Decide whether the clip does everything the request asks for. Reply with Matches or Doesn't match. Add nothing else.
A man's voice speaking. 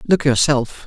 Matches